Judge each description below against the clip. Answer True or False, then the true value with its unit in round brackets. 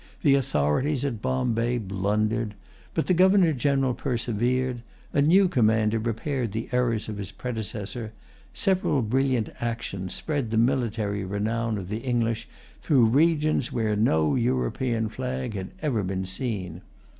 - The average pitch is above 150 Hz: False (115 Hz)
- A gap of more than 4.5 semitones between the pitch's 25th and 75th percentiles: False (3.6 semitones)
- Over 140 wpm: False (135 wpm)